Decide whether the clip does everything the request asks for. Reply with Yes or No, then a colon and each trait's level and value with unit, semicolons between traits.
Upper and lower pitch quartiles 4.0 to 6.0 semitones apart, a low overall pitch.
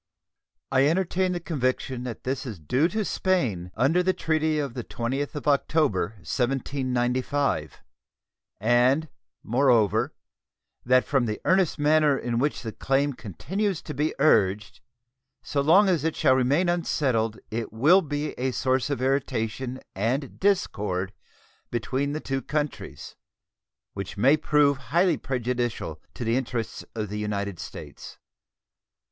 Yes: average, 4.6 semitones; low, 130 Hz